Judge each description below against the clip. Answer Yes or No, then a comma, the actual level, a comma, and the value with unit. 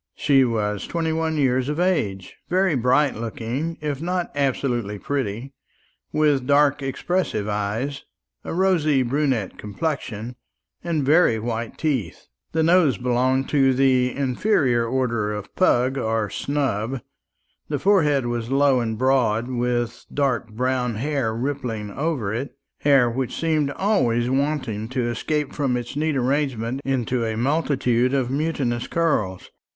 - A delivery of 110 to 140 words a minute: Yes, slow, 135 wpm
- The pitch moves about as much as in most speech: Yes, average, 3.9 semitones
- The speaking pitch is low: Yes, low, 130 Hz